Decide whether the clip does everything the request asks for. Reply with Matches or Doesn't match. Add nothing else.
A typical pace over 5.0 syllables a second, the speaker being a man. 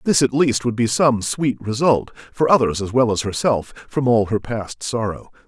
Doesn't match